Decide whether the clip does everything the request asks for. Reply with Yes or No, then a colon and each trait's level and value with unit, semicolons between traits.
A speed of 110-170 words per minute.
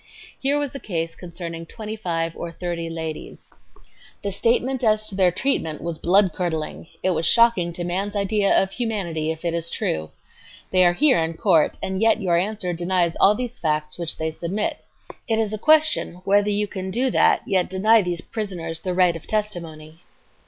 No: average, 190 wpm